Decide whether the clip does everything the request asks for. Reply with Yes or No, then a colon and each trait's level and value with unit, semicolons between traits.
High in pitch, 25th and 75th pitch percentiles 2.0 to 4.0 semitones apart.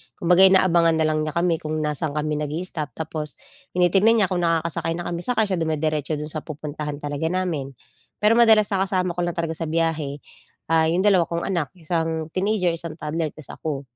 No: medium, 165 Hz; average, 2.7 semitones